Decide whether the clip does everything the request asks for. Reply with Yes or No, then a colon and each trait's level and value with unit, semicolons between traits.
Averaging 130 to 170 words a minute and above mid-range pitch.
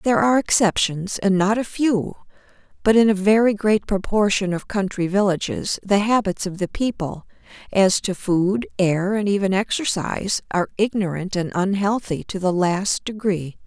Yes: average, 160 wpm; high, 195 Hz